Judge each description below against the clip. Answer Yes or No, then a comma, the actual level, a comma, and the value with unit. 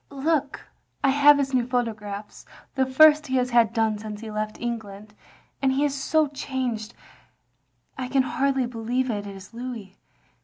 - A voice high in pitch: Yes, very high, 250 Hz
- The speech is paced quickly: No, average, 165 wpm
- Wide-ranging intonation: No, average, 3.8 semitones